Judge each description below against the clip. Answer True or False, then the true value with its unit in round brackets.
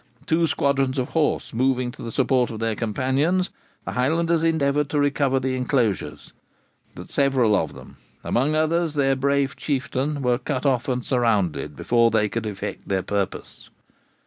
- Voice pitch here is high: False (130 Hz)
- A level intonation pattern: False (3.5 semitones)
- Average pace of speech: True (160 wpm)